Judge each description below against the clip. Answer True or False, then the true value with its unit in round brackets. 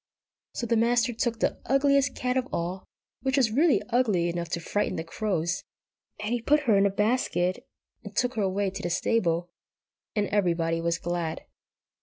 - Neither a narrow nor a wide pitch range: False (5.8 semitones)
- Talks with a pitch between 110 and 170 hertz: False (205 Hz)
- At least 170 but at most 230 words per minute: True (180 wpm)